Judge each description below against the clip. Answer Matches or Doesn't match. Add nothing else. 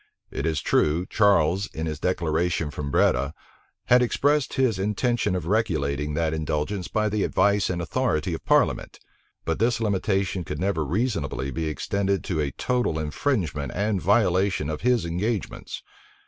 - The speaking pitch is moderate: Doesn't match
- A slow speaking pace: Doesn't match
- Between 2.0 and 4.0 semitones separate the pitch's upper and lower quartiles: Doesn't match